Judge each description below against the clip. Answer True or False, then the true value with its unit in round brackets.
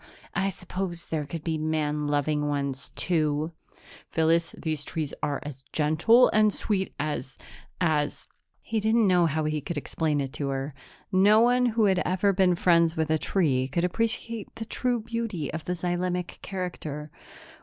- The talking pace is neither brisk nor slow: True (165 wpm)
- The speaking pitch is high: False (165 Hz)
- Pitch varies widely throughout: False (4.4 semitones)